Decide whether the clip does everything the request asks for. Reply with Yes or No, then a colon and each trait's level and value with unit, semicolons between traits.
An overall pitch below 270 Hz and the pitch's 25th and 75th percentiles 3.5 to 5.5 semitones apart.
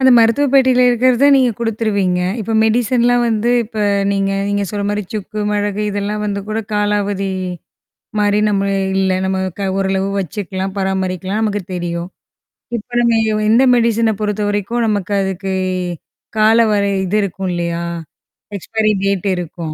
No: high, 205 Hz; narrow, 2.5 semitones